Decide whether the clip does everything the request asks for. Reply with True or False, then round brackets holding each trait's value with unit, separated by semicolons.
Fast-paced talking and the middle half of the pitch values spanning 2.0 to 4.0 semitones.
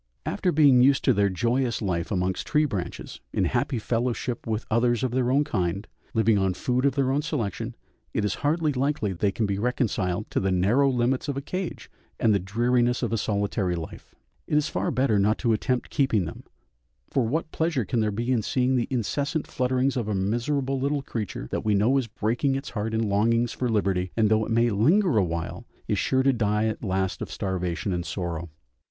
False (210 wpm; 4.6 semitones)